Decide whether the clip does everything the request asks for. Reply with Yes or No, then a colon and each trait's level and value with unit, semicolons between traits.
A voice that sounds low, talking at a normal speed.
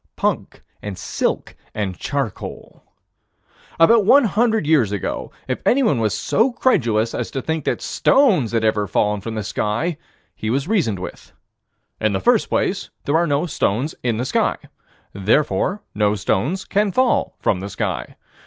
Yes: low, 130 Hz; average, 160 wpm